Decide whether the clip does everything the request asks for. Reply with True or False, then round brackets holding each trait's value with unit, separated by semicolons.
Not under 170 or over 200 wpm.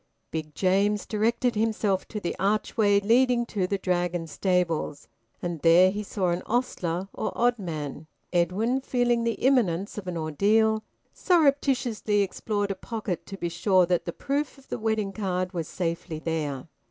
False (155 wpm)